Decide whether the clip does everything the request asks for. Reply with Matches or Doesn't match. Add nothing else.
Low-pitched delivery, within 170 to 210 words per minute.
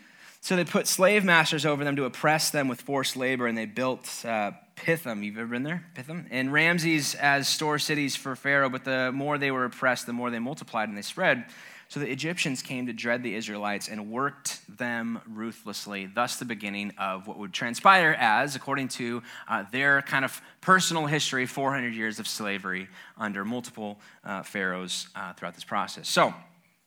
Matches